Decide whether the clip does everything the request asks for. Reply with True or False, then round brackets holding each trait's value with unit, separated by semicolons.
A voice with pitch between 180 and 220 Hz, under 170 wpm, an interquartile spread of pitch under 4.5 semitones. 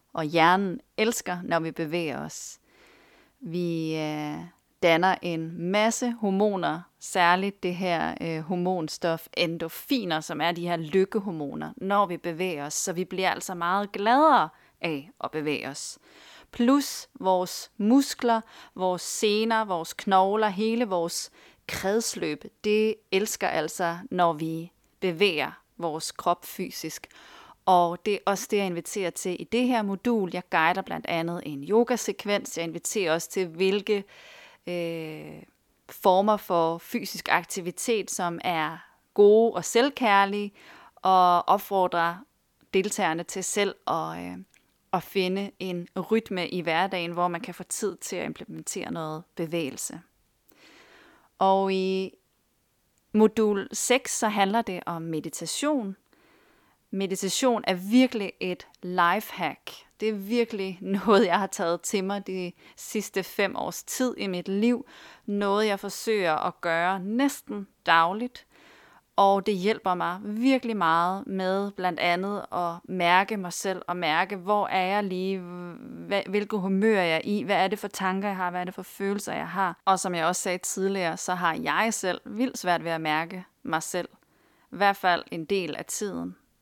True (190 Hz; 145 wpm; 3.5 semitones)